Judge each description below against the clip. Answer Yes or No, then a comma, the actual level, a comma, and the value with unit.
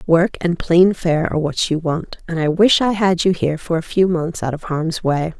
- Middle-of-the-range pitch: Yes, medium, 170 Hz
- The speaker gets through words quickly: Yes, fast, 255 wpm